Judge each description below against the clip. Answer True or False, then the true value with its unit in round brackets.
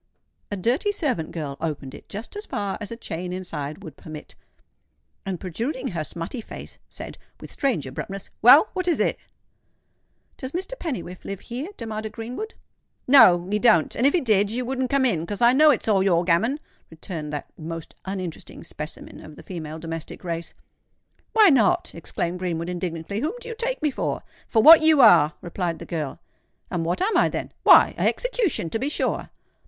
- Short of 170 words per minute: False (180 wpm)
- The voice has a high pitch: True (200 Hz)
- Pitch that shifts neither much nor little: False (8.0 semitones)